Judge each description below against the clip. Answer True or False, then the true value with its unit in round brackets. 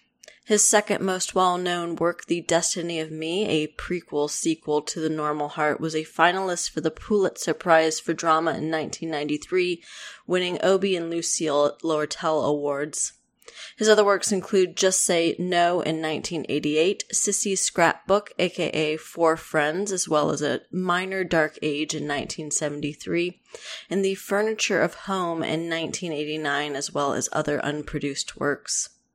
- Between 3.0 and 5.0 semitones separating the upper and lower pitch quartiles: True (3.5 semitones)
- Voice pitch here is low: False (165 Hz)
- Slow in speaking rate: False (145 wpm)